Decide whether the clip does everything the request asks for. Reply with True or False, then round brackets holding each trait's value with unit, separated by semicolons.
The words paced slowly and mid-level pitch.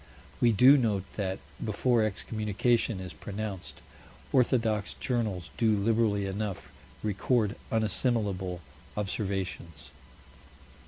False (90 wpm; 105 Hz)